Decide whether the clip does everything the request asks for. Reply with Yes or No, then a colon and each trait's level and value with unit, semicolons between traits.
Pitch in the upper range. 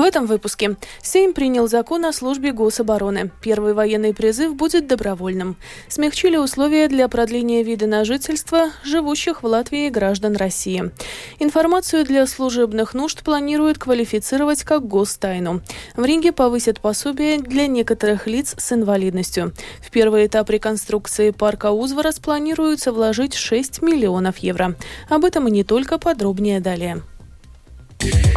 Yes: high, 235 Hz